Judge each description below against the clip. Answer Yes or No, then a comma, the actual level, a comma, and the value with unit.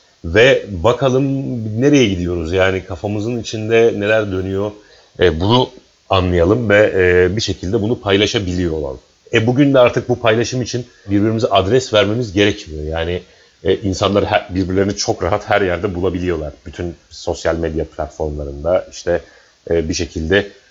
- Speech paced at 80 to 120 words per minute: No, fast, 140 wpm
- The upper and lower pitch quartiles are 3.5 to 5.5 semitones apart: Yes, average, 4.4 semitones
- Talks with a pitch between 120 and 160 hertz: No, low, 100 Hz